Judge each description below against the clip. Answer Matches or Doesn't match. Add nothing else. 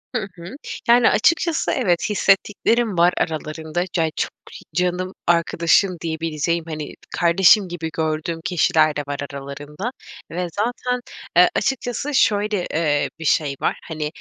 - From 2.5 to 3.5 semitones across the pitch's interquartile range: Doesn't match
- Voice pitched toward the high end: Doesn't match